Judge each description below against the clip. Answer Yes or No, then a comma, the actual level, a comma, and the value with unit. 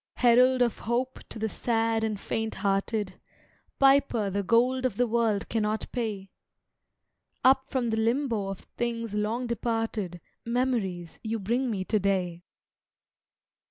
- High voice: Yes, high, 225 Hz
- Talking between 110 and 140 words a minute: Yes, slow, 135 wpm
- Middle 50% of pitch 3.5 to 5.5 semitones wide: No, average, 3.1 semitones